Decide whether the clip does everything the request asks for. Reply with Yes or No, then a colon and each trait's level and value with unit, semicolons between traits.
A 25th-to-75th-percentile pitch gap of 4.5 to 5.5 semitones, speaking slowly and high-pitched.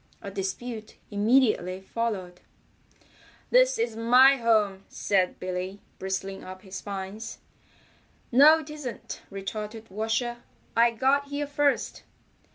Yes: average, 4.9 semitones; slow, 110 wpm; high, 220 Hz